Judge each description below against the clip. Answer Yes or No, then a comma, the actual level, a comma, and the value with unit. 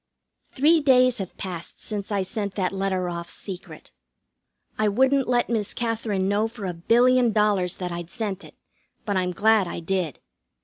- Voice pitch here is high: Yes, high, 200 Hz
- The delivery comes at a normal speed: Yes, average, 170 wpm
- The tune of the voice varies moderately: Yes, average, 3.8 semitones